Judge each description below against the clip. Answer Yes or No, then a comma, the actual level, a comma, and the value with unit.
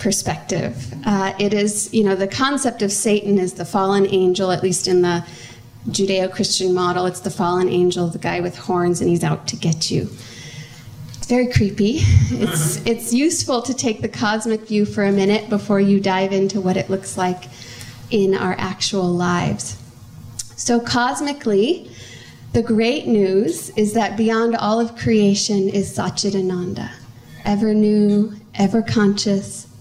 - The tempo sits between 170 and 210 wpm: No, average, 155 wpm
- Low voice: No, high, 195 Hz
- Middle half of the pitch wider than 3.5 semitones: No, average, 3.1 semitones